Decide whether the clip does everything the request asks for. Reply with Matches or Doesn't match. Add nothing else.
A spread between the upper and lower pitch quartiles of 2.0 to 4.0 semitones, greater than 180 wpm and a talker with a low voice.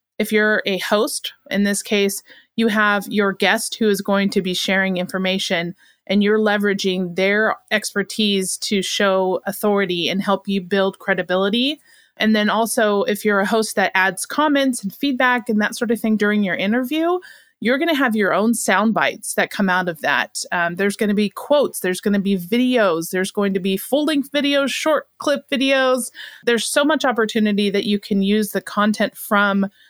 Doesn't match